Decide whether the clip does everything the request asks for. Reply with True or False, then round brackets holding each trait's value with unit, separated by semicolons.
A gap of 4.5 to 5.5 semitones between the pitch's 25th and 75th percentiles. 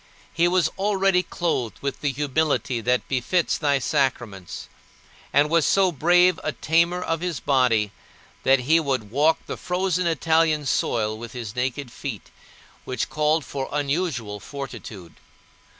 True (5.0 semitones)